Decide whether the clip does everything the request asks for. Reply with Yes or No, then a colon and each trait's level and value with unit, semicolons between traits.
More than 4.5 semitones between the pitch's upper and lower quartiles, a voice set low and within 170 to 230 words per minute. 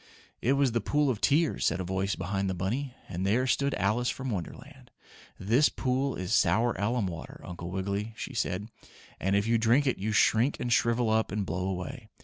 Yes: average, 4.9 semitones; low, 110 Hz; average, 200 wpm